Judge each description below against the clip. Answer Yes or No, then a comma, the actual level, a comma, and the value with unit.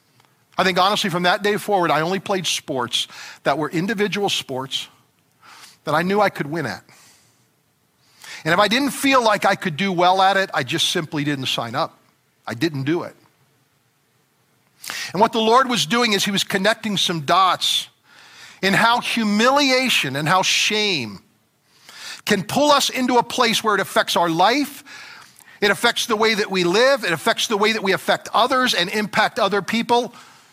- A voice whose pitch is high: Yes, high, 200 Hz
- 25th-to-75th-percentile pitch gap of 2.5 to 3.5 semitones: No, average, 5.3 semitones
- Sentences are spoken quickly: No, average, 180 wpm